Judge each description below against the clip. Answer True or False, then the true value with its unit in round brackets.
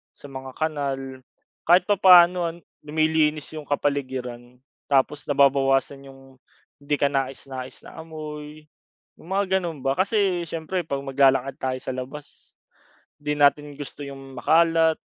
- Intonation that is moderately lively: True (3.1 semitones)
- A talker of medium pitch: True (145 Hz)